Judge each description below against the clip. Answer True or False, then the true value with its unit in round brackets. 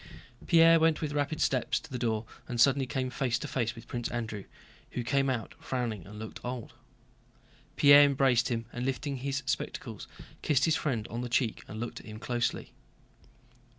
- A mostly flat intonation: False (3.1 semitones)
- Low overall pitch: True (125 Hz)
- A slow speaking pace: False (185 wpm)